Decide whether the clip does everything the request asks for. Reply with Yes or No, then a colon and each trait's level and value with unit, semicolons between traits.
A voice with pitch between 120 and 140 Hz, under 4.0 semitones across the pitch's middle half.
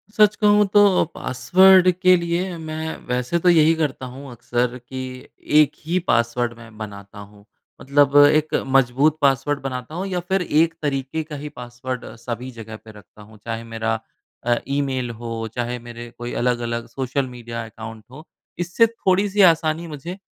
No: low, 135 Hz; wide, 5.5 semitones